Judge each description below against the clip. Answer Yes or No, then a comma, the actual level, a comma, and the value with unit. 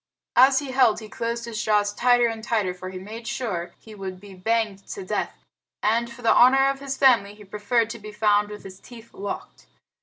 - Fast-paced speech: Yes, fast, 215 wpm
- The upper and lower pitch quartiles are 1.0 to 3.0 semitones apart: Yes, average, 2.7 semitones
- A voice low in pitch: No, high, 220 Hz